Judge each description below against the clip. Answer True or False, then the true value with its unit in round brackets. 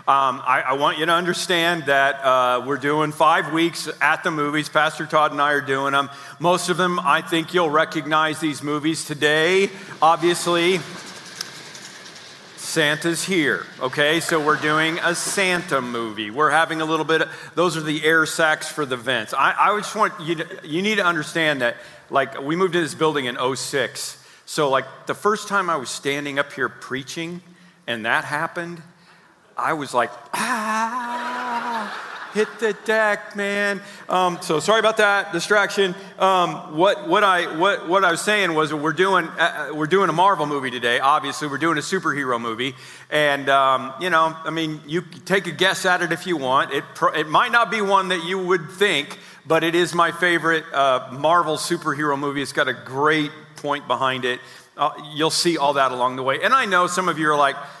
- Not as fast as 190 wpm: False (195 wpm)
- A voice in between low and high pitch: True (160 Hz)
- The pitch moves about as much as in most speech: True (3.5 semitones)